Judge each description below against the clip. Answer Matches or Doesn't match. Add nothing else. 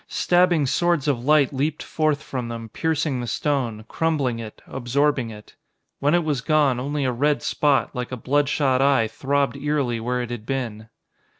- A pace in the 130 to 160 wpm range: Doesn't match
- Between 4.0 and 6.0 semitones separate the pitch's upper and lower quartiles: Doesn't match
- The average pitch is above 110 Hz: Matches